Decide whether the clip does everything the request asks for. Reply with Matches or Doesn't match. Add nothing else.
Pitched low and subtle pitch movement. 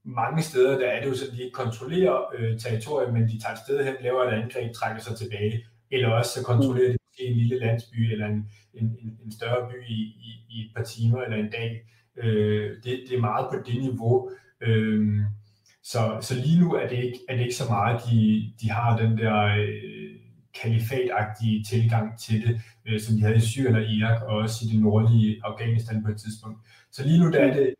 Matches